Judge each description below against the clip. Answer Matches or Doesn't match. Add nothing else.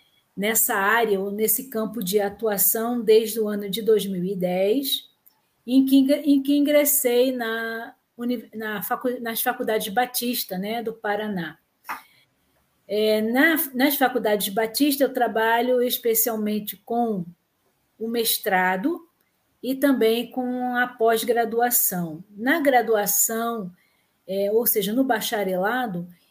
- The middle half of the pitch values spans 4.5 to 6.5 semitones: Doesn't match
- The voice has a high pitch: Matches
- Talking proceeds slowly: Matches